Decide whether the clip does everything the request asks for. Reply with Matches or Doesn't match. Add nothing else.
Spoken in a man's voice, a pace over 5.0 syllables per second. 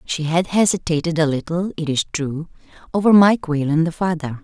Doesn't match